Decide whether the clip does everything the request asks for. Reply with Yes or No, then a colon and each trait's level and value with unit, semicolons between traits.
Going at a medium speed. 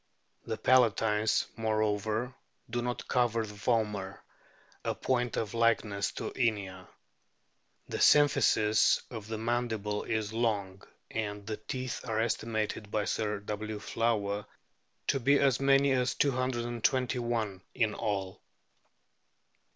No: slow, 120 wpm